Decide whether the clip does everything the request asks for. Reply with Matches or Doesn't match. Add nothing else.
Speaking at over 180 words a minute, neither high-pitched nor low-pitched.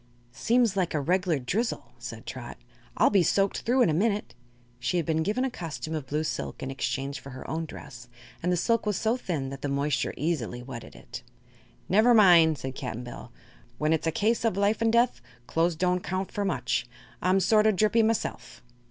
Matches